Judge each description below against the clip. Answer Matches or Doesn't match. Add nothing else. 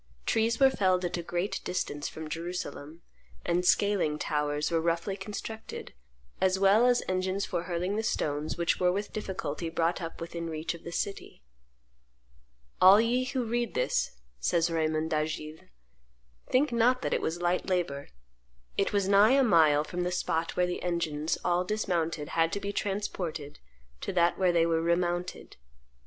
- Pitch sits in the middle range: Matches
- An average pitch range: Matches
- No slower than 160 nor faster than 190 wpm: Matches